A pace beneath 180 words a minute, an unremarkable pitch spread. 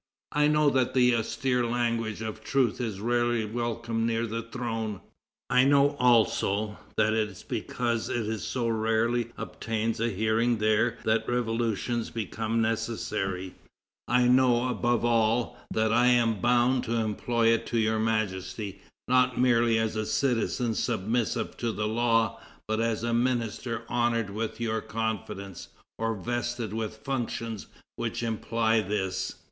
No: average, 140 wpm; narrow, 1.7 semitones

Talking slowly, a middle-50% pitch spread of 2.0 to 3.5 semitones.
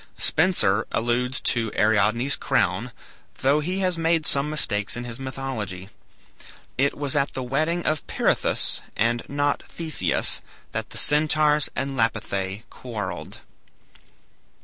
No: slow, 125 wpm; average, 5.2 semitones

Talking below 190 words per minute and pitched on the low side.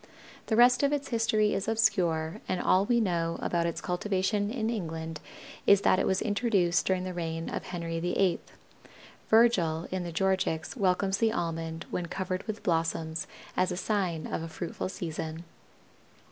No: average, 165 wpm; medium, 185 Hz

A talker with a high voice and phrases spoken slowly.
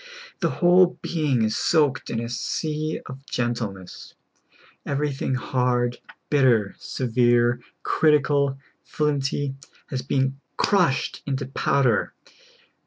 No: low, 135 Hz; slow, 100 wpm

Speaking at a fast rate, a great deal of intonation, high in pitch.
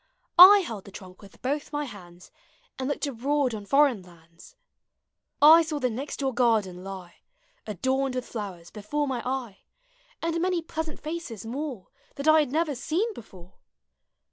No: average, 160 wpm; wide, 6.7 semitones; very high, 260 Hz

